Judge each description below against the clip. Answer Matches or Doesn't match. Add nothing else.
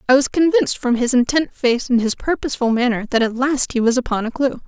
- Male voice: Doesn't match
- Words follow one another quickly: Matches